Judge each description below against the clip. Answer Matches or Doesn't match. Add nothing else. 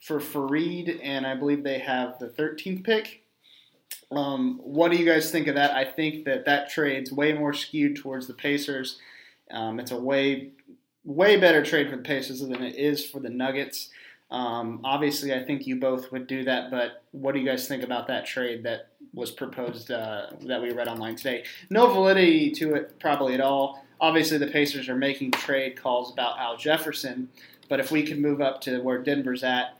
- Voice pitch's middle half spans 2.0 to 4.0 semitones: Matches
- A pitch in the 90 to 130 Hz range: Doesn't match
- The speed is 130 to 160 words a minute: Doesn't match